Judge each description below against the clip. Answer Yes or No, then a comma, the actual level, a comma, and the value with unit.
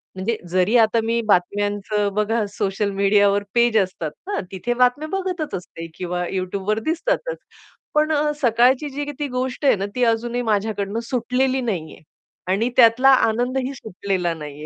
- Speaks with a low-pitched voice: No, high, 225 Hz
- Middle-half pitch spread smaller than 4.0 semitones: No, average, 4.3 semitones